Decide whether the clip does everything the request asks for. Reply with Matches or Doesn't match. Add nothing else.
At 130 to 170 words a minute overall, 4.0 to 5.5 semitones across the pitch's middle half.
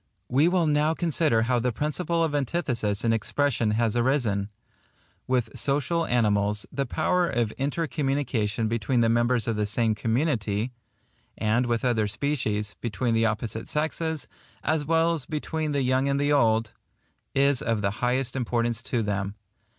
Matches